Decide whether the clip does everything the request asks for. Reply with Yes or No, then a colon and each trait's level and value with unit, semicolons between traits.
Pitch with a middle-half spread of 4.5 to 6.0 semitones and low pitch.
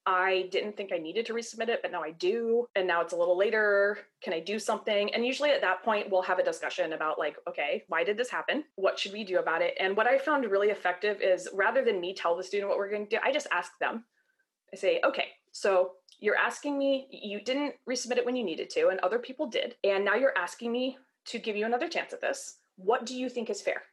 No: wide, 5.5 semitones; high, 220 Hz